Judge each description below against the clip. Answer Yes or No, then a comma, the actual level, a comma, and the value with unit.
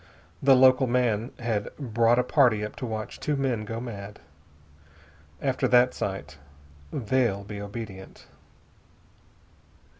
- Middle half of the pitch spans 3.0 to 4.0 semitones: Yes, average, 3.4 semitones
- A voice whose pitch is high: No, low, 115 Hz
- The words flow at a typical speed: No, slow, 120 wpm